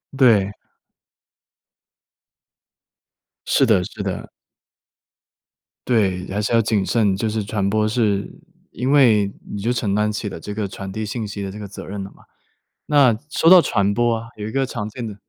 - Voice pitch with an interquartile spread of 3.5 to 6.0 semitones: No, narrow, 2.5 semitones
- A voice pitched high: No, low, 105 Hz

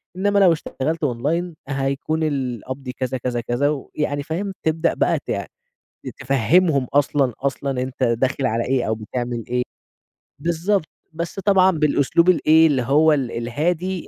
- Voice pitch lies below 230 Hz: Yes, medium, 140 Hz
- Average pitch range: Yes, average, 4.4 semitones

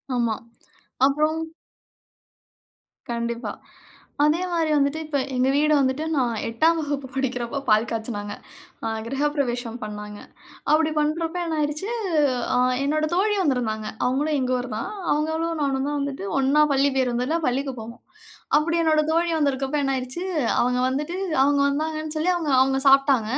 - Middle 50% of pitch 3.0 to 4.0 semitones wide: Yes, average, 3.7 semitones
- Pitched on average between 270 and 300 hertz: Yes, very high, 280 Hz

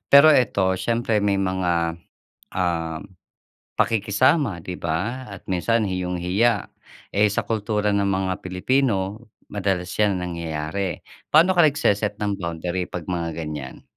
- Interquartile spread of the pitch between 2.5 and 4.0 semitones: Yes, average, 3.2 semitones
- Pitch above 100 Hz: No, very low, 95 Hz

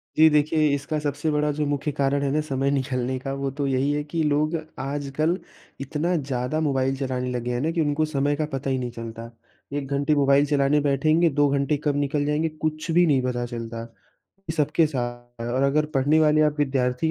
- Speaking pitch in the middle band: Yes, medium, 145 Hz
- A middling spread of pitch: No, narrow, 2.3 semitones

